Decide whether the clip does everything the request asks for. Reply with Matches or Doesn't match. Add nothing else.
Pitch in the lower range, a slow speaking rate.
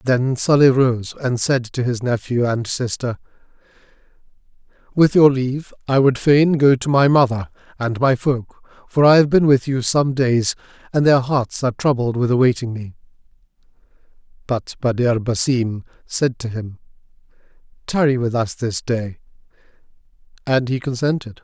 Doesn't match